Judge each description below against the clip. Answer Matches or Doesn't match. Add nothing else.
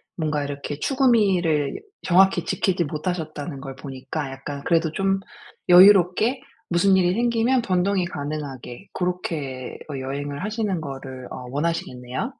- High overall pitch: Doesn't match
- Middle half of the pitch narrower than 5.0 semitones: Doesn't match